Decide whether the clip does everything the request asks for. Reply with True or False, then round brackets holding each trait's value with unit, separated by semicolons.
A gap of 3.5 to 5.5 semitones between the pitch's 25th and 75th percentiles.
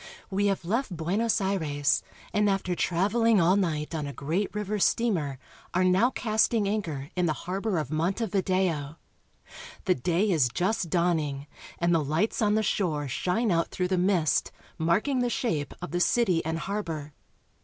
True (4.5 semitones)